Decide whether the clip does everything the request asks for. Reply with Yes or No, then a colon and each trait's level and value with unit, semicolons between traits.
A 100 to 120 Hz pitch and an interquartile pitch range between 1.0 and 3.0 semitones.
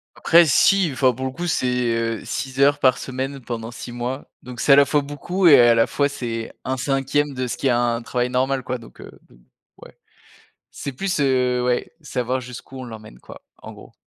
No: low, 130 Hz; narrow, 2.5 semitones